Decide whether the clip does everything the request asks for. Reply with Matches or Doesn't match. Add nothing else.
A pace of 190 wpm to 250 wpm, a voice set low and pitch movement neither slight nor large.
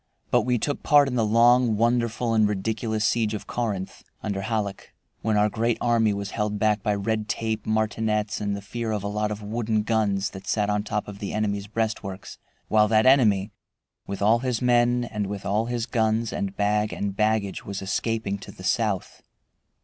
Doesn't match